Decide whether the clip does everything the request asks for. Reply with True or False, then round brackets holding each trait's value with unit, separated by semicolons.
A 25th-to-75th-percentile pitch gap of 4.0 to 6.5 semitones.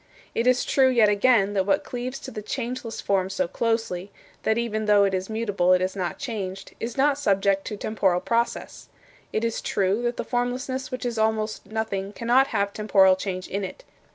False (3.6 semitones)